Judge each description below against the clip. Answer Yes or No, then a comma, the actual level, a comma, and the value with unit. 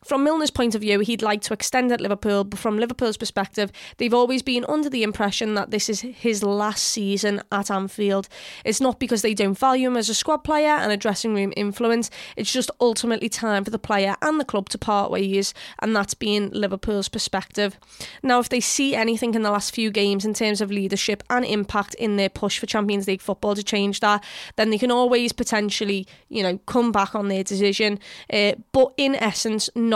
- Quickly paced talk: Yes, fast, 210 wpm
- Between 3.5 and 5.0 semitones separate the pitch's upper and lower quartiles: No, average, 2.7 semitones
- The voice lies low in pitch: No, high, 215 Hz